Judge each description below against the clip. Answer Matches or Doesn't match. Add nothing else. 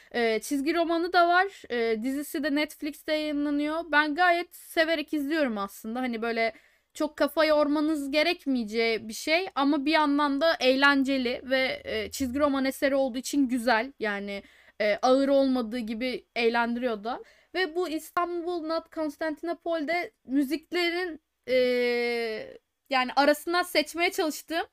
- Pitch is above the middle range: Matches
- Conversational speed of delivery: Matches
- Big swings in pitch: Doesn't match